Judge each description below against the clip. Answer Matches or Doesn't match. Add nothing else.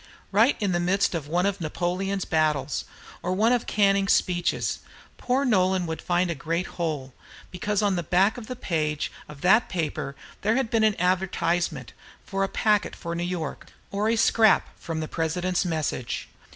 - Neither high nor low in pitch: Matches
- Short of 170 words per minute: Doesn't match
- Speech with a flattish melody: Doesn't match